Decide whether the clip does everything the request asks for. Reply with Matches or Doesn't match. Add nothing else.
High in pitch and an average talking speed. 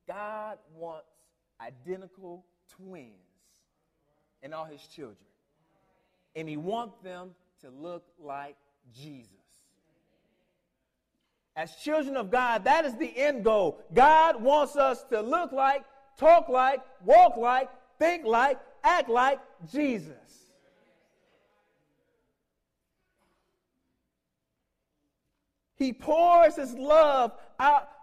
Doesn't match